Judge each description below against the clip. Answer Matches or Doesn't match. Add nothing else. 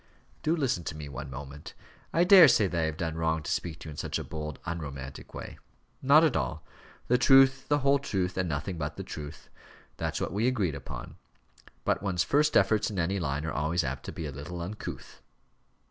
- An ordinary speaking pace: Doesn't match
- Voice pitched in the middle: Doesn't match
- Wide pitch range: Matches